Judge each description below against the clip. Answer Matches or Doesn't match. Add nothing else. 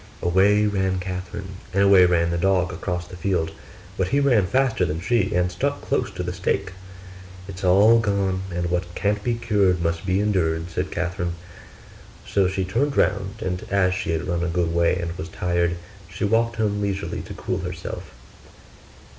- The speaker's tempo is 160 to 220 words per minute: Matches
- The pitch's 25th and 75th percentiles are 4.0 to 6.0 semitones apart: Doesn't match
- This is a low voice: Matches